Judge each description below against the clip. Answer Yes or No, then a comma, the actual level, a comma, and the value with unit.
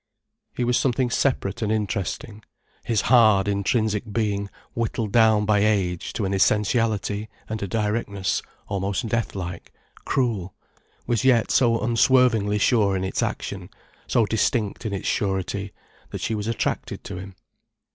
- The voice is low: Yes, low, 105 Hz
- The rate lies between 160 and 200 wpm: No, average, 145 wpm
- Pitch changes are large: No, average, 2.7 semitones